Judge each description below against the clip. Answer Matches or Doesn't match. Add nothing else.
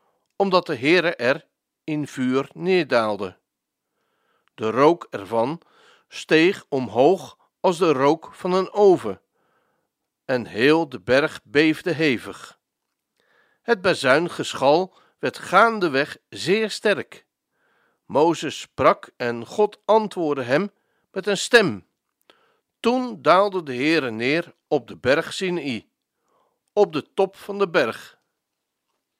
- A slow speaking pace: Matches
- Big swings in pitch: Matches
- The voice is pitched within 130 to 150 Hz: Doesn't match